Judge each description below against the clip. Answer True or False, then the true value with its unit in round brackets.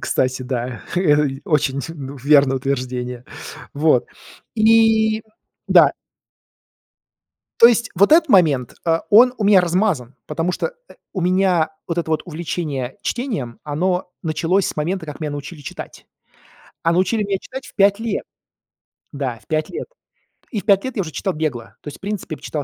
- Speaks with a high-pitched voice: False (165 Hz)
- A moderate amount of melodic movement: False (6.1 semitones)